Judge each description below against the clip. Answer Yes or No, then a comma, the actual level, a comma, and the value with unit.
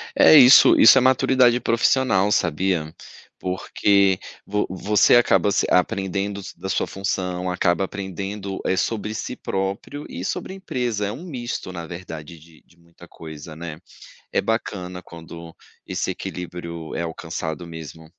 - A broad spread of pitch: No, average, 3.7 semitones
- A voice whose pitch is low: Yes, very low, 95 Hz